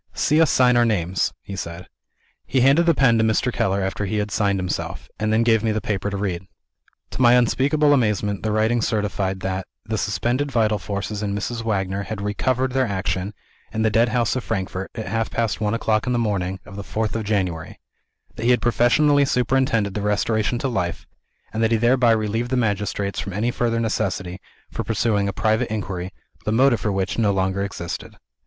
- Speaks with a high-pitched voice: No, low, 110 Hz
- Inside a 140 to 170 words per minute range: No, average, 200 wpm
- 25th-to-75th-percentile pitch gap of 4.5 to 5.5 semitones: No, average, 3.2 semitones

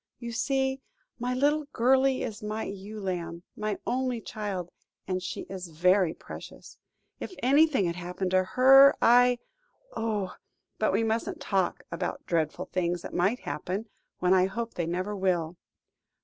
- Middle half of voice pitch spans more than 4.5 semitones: Yes, average, 5.3 semitones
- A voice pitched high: Yes, high, 205 Hz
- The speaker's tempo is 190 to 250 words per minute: No, average, 150 wpm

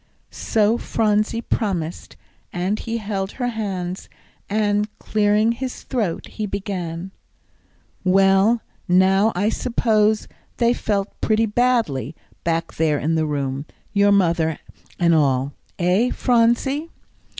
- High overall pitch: Yes, high, 200 Hz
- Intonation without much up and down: No, average, 4.3 semitones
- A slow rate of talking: Yes, slow, 115 wpm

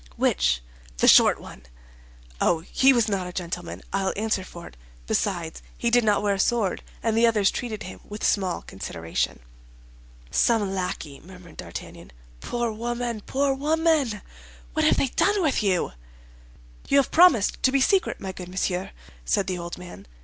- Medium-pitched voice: No, high, 200 Hz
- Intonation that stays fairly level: No, average, 5.0 semitones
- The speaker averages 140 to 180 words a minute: Yes, average, 165 wpm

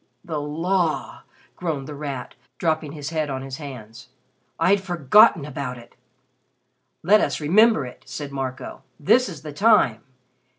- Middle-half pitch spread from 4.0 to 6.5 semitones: Yes, average, 4.3 semitones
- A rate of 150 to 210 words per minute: No, average, 140 wpm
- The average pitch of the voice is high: No, medium, 150 Hz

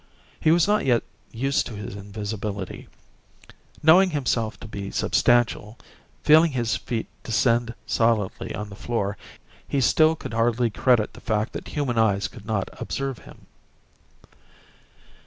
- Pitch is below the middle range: Yes, low, 115 Hz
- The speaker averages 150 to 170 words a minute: No, average, 140 wpm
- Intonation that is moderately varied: Yes, average, 4.0 semitones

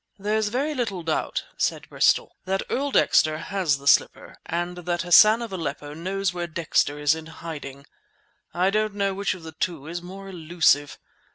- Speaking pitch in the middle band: Yes, medium, 175 Hz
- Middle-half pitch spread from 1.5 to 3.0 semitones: No, average, 3.7 semitones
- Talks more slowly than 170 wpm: No, average, 175 wpm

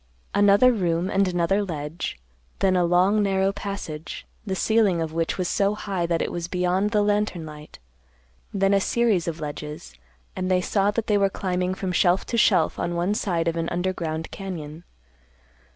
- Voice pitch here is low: No, medium, 185 Hz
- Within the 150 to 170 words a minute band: No, average, 180 wpm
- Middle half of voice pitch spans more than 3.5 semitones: No, average, 3.0 semitones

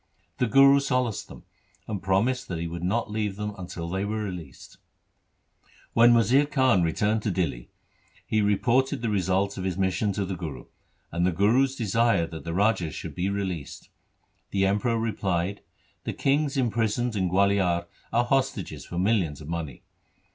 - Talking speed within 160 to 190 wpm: Yes, average, 170 wpm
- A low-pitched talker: Yes, low, 100 Hz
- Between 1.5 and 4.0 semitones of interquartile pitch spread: No, average, 4.4 semitones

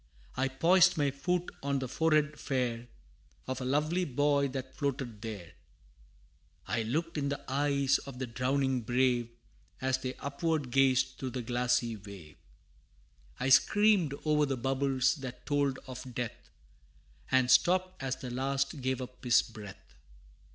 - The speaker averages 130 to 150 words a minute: Yes, average, 145 wpm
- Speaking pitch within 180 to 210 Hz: No, low, 130 Hz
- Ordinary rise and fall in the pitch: No, narrow, 2.3 semitones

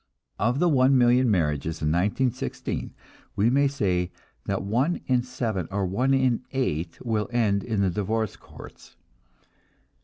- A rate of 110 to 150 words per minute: Yes, average, 145 wpm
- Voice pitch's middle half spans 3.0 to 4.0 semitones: No, average, 5.2 semitones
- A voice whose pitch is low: Yes, low, 110 Hz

